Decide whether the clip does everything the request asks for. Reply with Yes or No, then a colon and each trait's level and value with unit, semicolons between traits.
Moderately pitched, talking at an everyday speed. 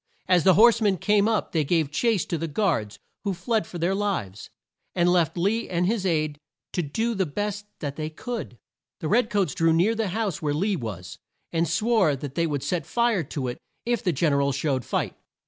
No: medium, 175 Hz; fast, 215 wpm